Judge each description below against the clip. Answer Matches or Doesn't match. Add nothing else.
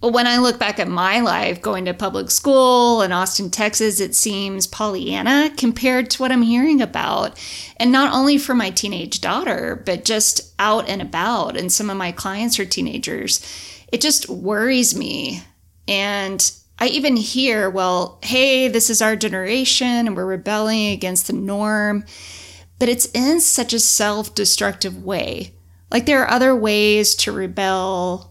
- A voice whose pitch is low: Doesn't match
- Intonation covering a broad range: Doesn't match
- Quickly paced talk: Doesn't match